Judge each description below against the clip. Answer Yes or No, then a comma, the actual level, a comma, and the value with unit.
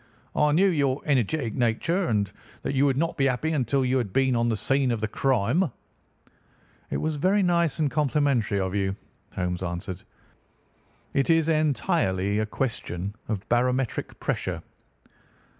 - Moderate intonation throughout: No, wide, 5.9 semitones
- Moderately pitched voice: No, low, 130 Hz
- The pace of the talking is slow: No, average, 155 wpm